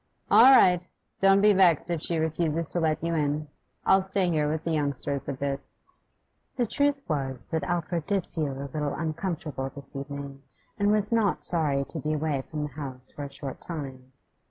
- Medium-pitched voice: Yes, medium, 155 Hz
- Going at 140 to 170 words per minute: No, average, 190 wpm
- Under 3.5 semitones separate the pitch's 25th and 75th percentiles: No, average, 3.8 semitones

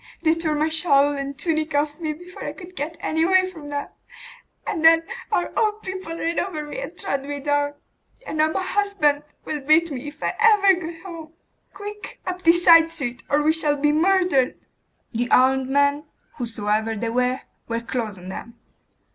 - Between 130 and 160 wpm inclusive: No, average, 185 wpm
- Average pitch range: Yes, average, 3.6 semitones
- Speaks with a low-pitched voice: No, very high, 310 Hz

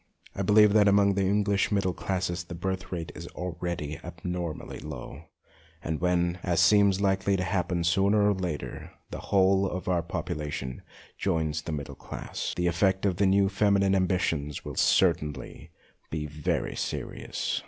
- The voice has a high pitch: No, very low, 90 Hz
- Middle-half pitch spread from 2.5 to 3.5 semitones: Yes, average, 3.1 semitones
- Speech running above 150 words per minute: Yes, average, 175 wpm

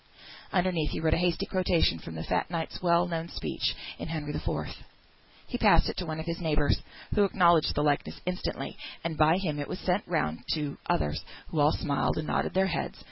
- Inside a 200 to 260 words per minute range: Yes, fast, 205 wpm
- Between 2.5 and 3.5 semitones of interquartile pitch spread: Yes, average, 3.2 semitones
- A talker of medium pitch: Yes, medium, 160 Hz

